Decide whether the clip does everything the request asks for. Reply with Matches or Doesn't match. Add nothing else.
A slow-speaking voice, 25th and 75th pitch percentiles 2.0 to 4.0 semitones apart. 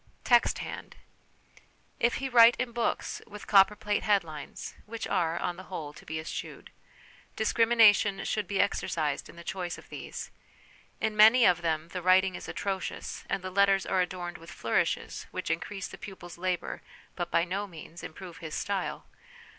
Doesn't match